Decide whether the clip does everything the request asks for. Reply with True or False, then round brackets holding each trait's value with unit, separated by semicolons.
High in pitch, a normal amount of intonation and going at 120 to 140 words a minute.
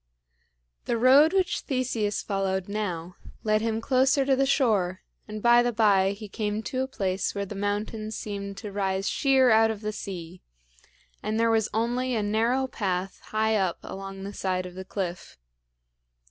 False (215 Hz; 3.4 semitones; 175 wpm)